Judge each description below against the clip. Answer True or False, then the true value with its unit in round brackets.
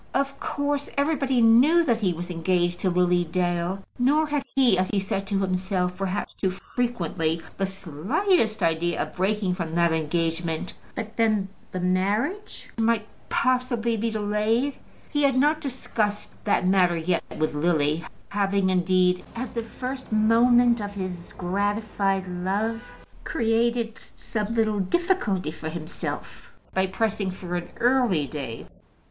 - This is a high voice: True (200 Hz)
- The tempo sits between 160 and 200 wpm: False (140 wpm)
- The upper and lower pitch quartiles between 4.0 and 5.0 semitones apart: True (4.7 semitones)